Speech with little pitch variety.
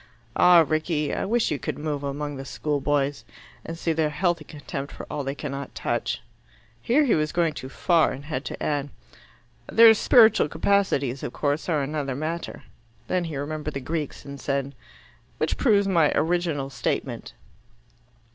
No: average, 3.4 semitones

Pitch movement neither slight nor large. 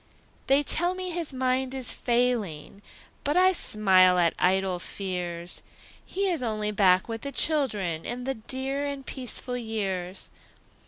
No: wide, 6.3 semitones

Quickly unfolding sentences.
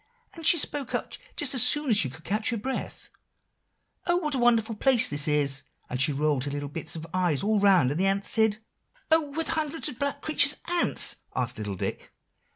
Yes: fast, 215 wpm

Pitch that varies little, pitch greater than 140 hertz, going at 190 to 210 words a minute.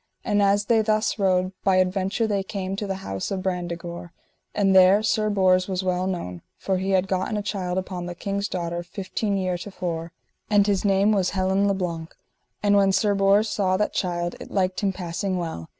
Yes: narrow, 1.8 semitones; high, 190 Hz; fast, 205 wpm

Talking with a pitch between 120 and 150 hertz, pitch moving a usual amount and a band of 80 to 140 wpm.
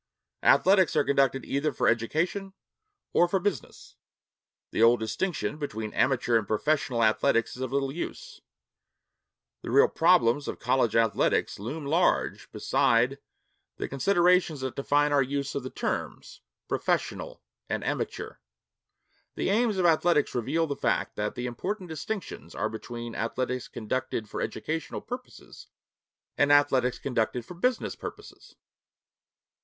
No: medium, 140 Hz; wide, 6.3 semitones; slow, 135 wpm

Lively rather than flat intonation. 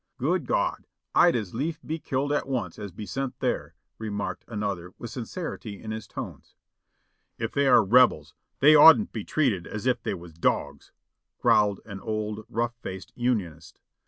No: average, 4.7 semitones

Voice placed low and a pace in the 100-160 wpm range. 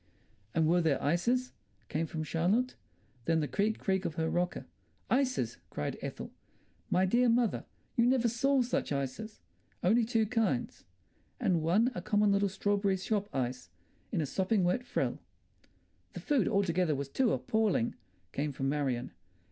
No: high, 190 Hz; average, 155 wpm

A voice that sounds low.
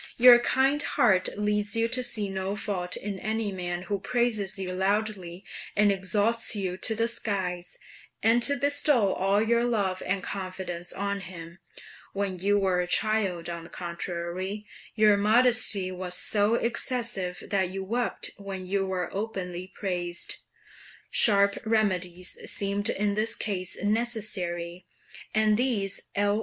No: high, 200 Hz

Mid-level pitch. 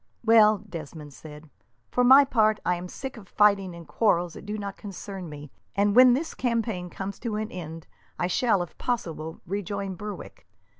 No: high, 200 Hz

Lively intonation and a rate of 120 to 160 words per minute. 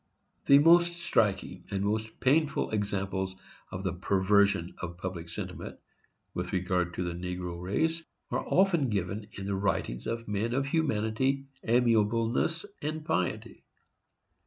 Yes: wide, 6.5 semitones; slow, 135 wpm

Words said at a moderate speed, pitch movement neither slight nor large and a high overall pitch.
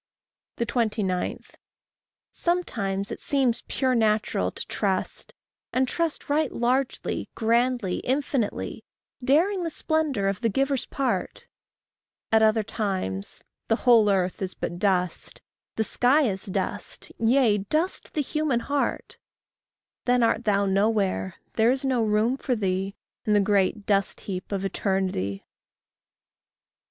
No: slow, 125 wpm; average, 5.0 semitones; high, 220 Hz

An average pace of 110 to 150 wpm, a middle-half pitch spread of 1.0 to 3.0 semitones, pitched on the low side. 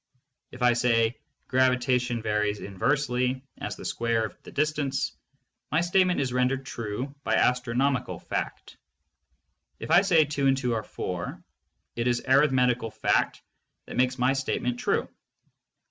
Yes: average, 140 wpm; narrow, 2.5 semitones; low, 125 Hz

